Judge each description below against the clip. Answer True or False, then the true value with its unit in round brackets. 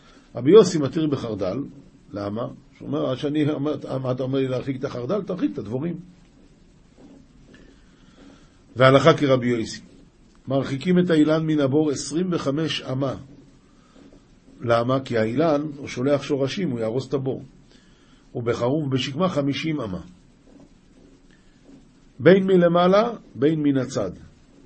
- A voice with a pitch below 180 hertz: True (140 Hz)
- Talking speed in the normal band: True (115 wpm)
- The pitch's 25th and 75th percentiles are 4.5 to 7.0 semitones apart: False (3.4 semitones)